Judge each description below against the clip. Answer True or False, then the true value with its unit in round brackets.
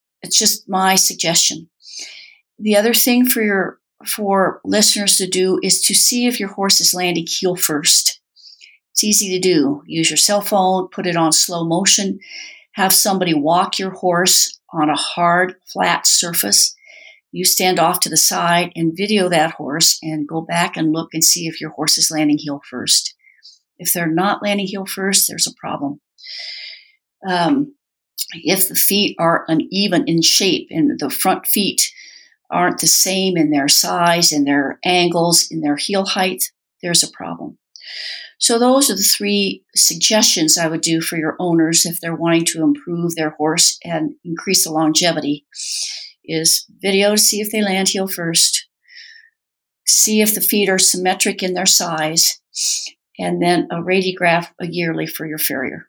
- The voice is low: False (185 Hz)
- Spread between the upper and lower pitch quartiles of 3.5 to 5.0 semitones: True (3.8 semitones)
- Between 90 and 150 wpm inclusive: False (170 wpm)